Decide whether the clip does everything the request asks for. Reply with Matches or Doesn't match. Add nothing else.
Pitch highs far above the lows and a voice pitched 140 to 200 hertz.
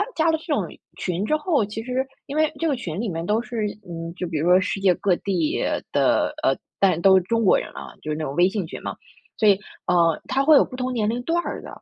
Doesn't match